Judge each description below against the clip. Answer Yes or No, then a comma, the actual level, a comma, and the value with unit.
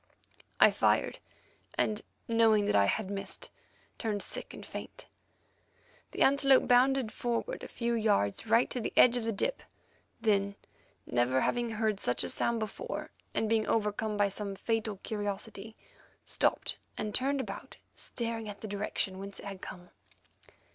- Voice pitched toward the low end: No, high, 215 Hz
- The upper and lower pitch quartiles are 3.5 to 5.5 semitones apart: No, narrow, 2.6 semitones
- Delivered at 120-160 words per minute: Yes, average, 155 wpm